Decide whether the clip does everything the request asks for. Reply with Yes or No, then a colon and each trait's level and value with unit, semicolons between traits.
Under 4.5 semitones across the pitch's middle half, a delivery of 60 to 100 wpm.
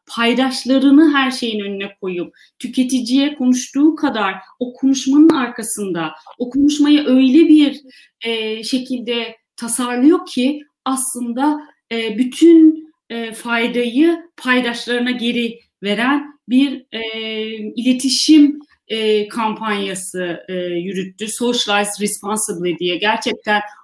Yes: average, 3.9 semitones; slow, 95 wpm